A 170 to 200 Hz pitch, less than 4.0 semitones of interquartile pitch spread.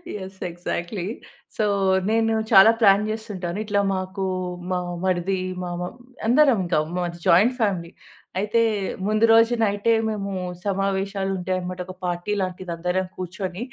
Yes: high, 195 Hz; average, 2.7 semitones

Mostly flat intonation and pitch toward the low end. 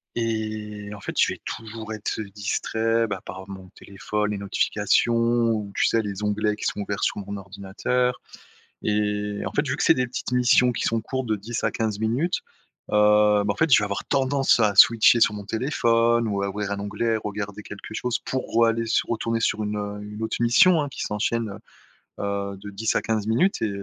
Yes: narrow, 2.2 semitones; low, 110 Hz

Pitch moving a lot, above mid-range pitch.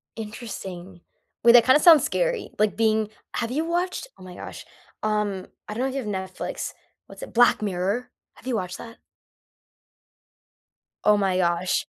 No: average, 4.9 semitones; high, 215 Hz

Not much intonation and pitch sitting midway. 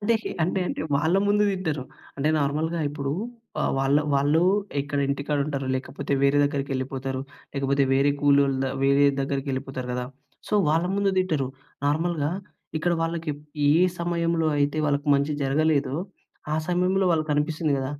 No: average, 3.0 semitones; medium, 145 Hz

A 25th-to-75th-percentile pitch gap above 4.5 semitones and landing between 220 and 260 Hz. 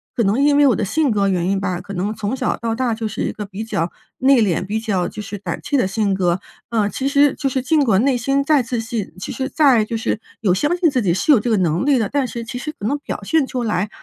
Yes: average, 5.3 semitones; high, 225 Hz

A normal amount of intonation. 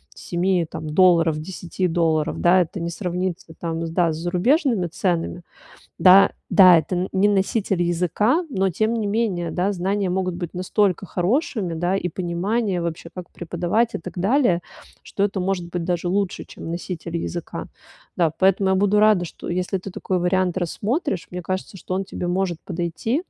No: narrow, 2.2 semitones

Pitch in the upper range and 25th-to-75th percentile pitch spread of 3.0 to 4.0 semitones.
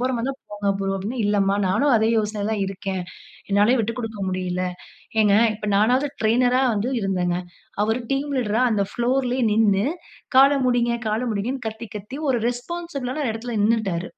Yes: high, 220 Hz; average, 3.6 semitones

